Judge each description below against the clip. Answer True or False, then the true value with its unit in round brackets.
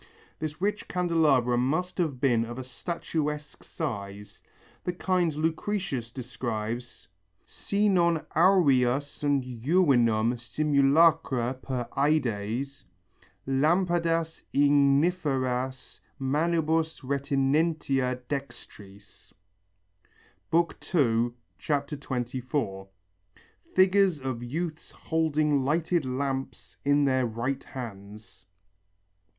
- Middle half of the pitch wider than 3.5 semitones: True (4.6 semitones)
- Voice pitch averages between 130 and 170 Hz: True (140 Hz)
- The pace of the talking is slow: True (80 wpm)